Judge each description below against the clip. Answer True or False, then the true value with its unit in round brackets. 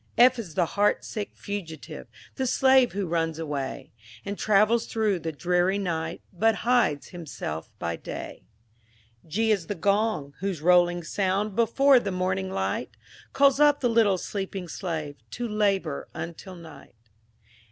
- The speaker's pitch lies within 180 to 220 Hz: True (190 Hz)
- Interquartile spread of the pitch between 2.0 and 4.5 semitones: False (4.9 semitones)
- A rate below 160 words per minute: True (145 wpm)